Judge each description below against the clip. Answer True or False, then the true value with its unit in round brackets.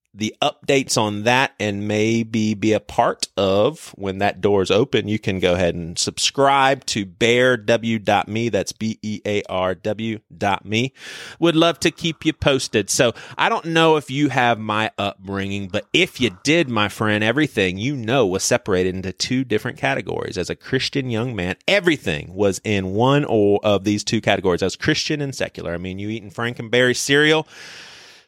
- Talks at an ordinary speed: True (175 wpm)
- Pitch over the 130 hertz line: False (110 Hz)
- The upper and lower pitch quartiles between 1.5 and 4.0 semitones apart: False (4.4 semitones)